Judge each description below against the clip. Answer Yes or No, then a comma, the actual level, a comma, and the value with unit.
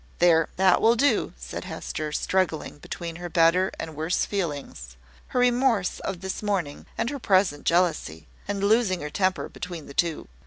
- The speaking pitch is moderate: Yes, medium, 180 Hz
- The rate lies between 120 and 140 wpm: No, average, 165 wpm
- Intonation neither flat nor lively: Yes, average, 4.2 semitones